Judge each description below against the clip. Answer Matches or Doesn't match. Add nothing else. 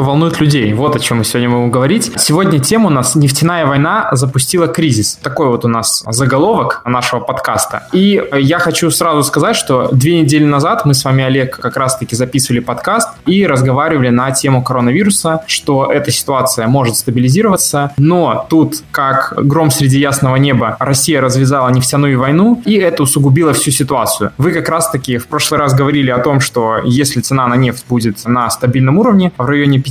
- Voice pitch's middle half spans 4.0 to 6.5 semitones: Doesn't match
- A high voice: Doesn't match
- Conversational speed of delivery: Doesn't match